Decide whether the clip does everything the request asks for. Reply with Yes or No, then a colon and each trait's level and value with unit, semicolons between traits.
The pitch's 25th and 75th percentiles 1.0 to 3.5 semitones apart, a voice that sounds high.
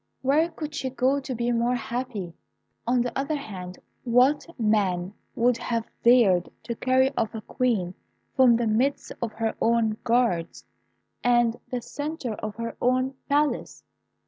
Yes: average, 2.8 semitones; high, 240 Hz